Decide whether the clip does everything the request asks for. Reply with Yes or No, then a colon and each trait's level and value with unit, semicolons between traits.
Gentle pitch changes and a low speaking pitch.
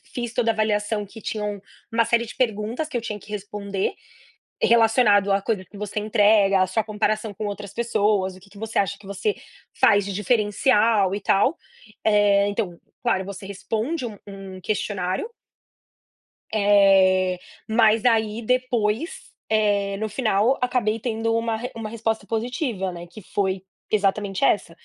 No: narrow, 2.2 semitones; high, 210 Hz